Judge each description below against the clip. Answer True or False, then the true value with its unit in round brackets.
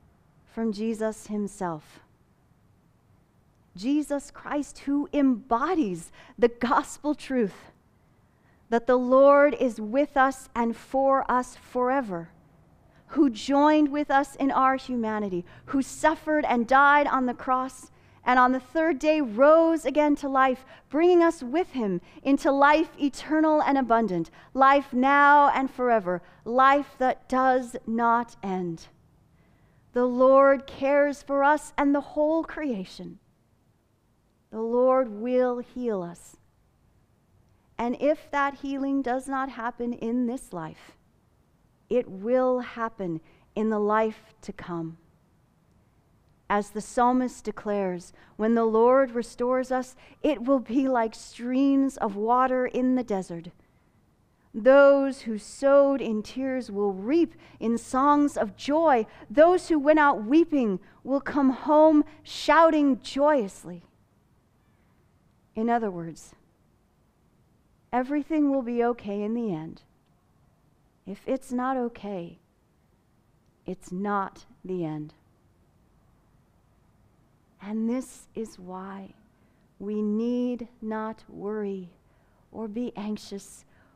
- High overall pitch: True (250 Hz)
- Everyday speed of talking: False (115 wpm)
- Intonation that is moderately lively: True (4.6 semitones)